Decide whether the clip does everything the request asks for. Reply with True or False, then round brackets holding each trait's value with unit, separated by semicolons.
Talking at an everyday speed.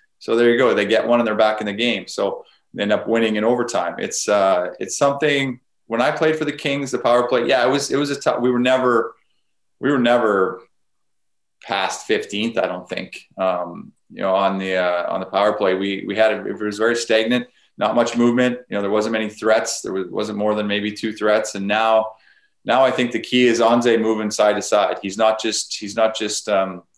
False (235 wpm)